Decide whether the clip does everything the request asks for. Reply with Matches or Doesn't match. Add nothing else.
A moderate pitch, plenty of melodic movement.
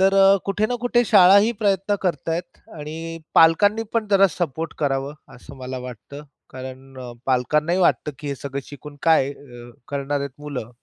Matches